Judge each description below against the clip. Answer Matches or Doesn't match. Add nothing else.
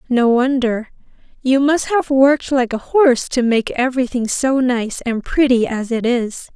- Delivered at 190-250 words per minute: Doesn't match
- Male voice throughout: Doesn't match